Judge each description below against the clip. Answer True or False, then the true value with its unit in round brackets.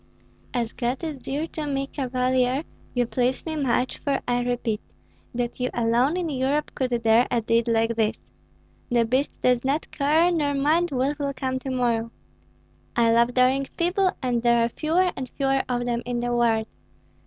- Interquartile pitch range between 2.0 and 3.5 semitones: True (2.8 semitones)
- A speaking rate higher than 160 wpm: True (180 wpm)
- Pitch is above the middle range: True (255 Hz)